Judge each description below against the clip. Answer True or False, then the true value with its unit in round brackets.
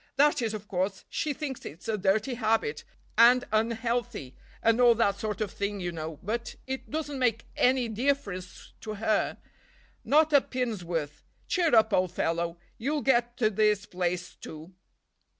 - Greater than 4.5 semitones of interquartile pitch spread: True (5.1 semitones)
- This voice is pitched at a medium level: False (220 Hz)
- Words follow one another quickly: False (160 wpm)